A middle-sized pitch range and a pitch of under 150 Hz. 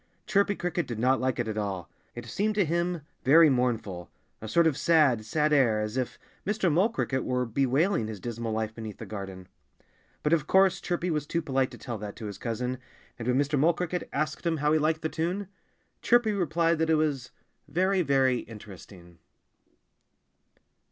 No: wide, 6.5 semitones; medium, 140 Hz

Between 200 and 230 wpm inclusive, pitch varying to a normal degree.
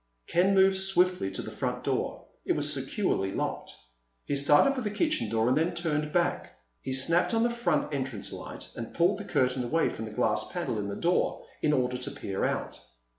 No: fast, 205 wpm; wide, 7.1 semitones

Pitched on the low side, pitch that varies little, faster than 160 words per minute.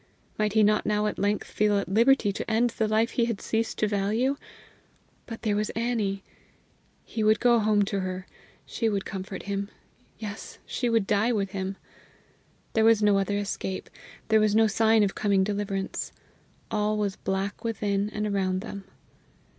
No: high, 210 Hz; narrow, 1.9 semitones; average, 175 wpm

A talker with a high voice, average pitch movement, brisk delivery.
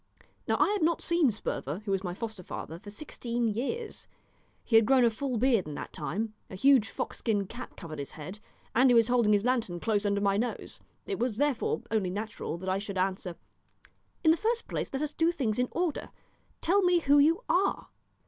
No: high, 230 Hz; wide, 6.1 semitones; fast, 215 wpm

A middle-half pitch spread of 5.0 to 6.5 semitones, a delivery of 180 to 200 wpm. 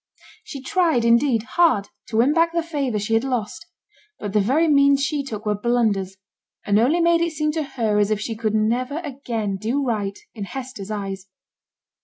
Yes: wide, 5.4 semitones; average, 190 wpm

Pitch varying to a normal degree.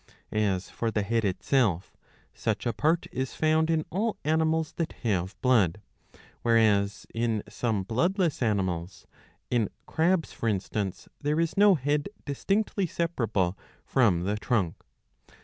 No: wide, 7.8 semitones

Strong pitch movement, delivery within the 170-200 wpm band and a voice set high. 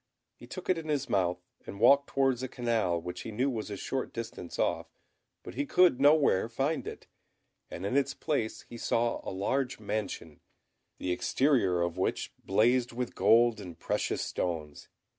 No: wide, 6.3 semitones; average, 175 wpm; low, 115 Hz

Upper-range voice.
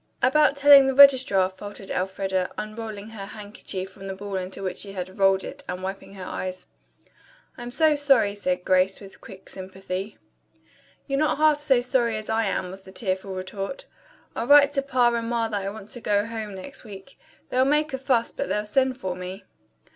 Yes: high, 210 Hz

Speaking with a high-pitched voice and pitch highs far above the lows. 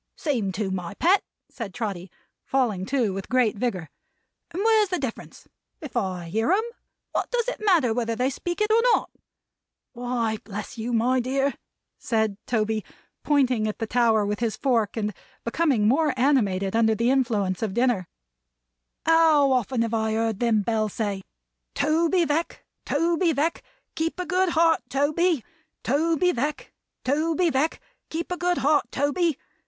Yes: very high, 250 Hz; wide, 6.6 semitones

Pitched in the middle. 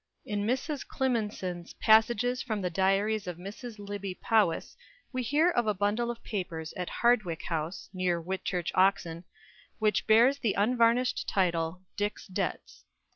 No: high, 205 Hz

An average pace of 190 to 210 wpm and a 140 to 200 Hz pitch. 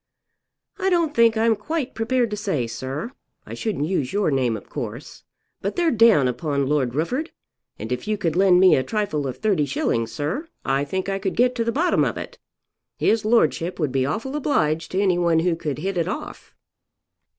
Yes: average, 195 wpm; high, 190 Hz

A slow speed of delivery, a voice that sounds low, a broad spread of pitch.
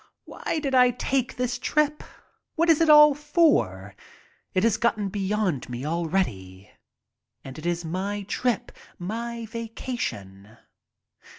No: slow, 125 wpm; high, 210 Hz; wide, 8.0 semitones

